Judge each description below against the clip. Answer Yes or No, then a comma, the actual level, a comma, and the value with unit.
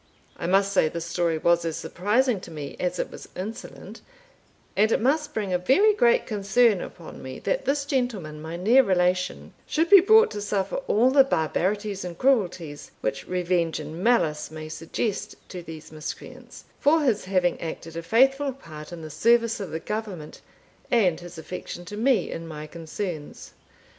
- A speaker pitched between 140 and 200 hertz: Yes, medium, 185 Hz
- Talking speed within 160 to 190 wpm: Yes, average, 175 wpm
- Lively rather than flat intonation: Yes, wide, 6.1 semitones